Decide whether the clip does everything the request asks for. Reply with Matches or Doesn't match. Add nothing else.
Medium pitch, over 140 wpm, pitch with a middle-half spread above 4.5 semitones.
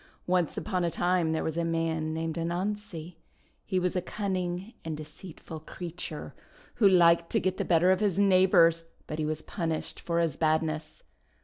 Doesn't match